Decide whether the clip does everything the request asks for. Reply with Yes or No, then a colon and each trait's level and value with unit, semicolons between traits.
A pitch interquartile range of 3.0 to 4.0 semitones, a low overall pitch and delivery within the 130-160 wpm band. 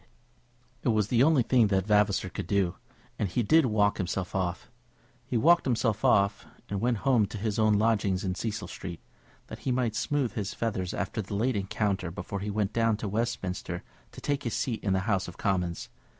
No: average, 3.3 semitones; low, 105 Hz; average, 200 wpm